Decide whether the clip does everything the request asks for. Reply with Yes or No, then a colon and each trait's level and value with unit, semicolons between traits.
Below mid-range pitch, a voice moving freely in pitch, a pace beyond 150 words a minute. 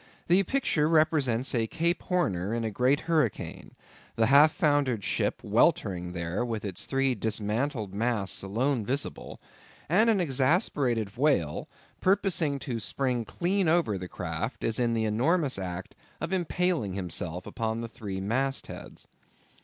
No: low, 125 Hz; wide, 6.6 semitones; average, 145 wpm